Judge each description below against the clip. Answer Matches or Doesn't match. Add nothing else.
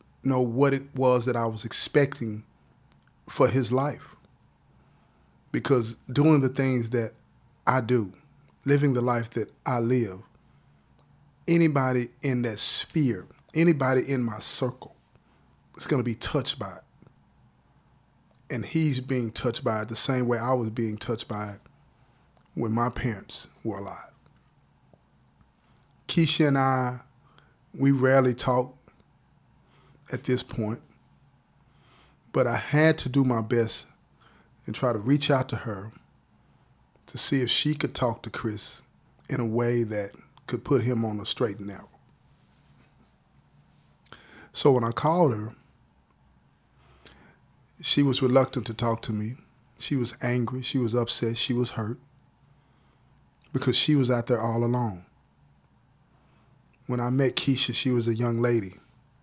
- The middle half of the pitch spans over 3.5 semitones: Doesn't match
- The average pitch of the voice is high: Doesn't match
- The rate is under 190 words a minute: Matches